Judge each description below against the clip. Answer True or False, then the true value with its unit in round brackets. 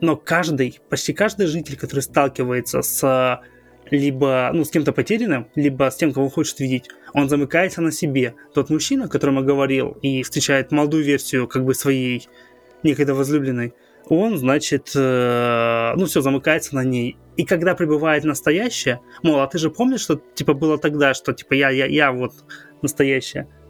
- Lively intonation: False (3.0 semitones)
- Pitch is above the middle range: False (140 Hz)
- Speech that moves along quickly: True (165 wpm)